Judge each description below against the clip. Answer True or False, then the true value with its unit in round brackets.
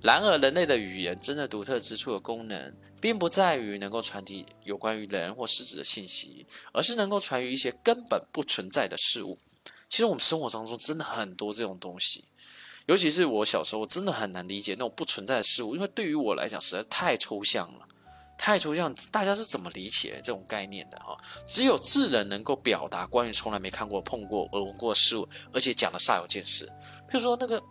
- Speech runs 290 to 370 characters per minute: True (330 characters per minute)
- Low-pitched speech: True (115 Hz)